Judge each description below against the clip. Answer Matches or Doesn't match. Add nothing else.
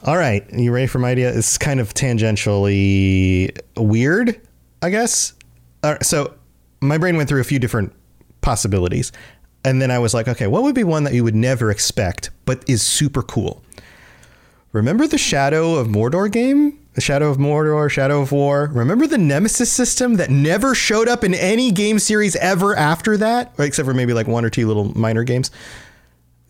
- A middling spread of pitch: Doesn't match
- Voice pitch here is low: Matches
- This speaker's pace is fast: Doesn't match